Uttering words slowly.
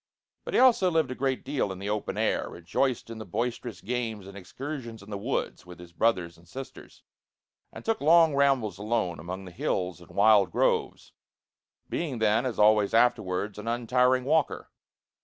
No: average, 175 wpm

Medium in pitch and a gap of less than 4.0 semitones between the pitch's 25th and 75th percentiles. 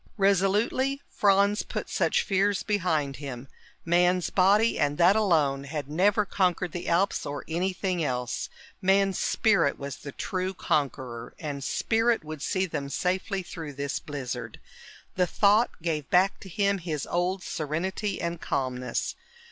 No: medium, 180 Hz; average, 5.2 semitones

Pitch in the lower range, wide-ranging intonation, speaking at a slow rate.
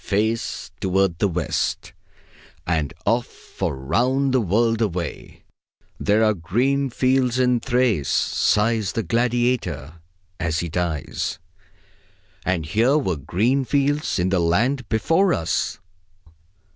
Yes: low, 110 Hz; wide, 6.4 semitones; slow, 120 wpm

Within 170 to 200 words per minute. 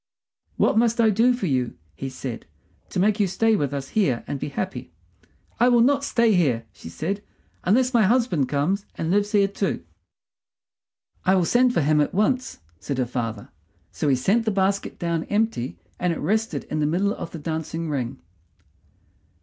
Yes: average, 185 wpm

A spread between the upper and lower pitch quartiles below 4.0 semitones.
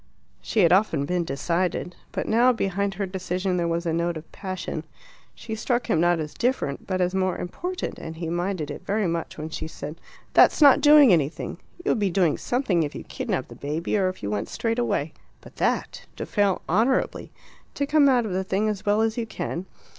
No: average, 4.5 semitones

